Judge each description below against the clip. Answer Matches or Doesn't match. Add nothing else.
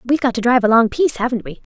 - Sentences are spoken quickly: Matches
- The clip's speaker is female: Matches